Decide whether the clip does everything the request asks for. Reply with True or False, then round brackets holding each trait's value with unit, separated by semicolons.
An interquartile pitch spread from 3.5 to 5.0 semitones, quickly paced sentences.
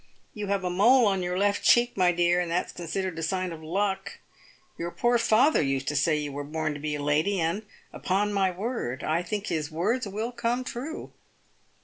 True (4.6 semitones; 210 wpm)